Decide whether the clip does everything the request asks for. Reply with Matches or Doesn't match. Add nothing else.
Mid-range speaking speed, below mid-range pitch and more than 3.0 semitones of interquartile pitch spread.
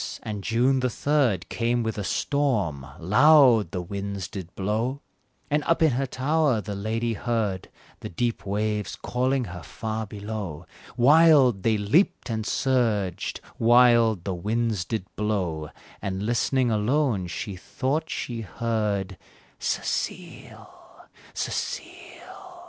Doesn't match